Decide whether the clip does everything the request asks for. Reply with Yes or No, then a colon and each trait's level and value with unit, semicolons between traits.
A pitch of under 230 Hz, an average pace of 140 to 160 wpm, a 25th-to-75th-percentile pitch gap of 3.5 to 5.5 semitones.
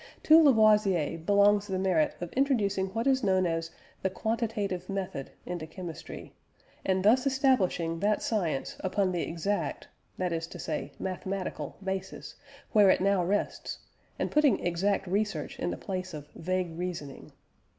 No: high, 190 Hz; average, 150 wpm; average, 3.0 semitones